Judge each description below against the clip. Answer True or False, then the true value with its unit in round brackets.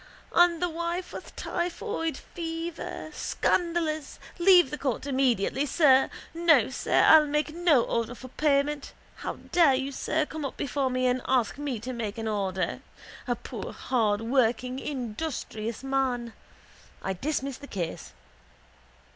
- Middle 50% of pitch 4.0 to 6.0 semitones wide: True (4.7 semitones)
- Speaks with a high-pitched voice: True (275 Hz)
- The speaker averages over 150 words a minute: False (140 wpm)